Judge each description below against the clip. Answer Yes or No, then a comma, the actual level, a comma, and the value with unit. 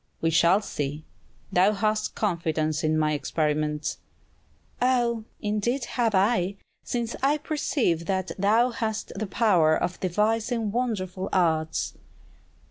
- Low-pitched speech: No, high, 195 Hz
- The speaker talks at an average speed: No, slow, 120 wpm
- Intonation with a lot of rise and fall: Yes, wide, 6.0 semitones